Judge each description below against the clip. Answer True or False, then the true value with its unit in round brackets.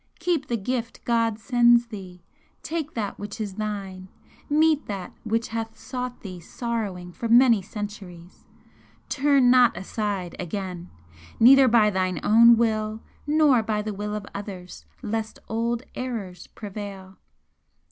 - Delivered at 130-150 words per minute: True (135 wpm)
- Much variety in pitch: False (3.4 semitones)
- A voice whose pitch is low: False (220 Hz)